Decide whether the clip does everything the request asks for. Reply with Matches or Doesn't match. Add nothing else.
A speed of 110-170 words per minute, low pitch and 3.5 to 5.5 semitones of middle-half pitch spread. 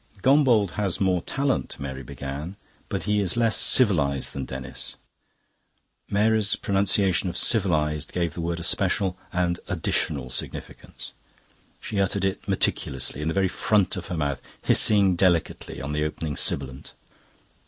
Matches